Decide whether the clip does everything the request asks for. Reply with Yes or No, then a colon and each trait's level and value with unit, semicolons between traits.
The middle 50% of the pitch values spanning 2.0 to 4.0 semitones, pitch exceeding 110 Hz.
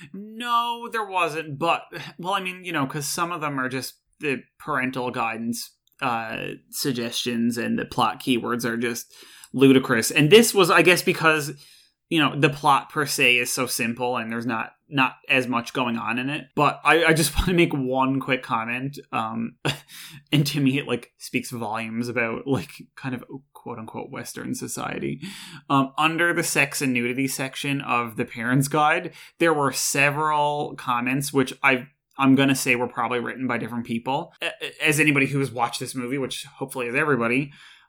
Yes: average, 3.6 semitones; low, 135 Hz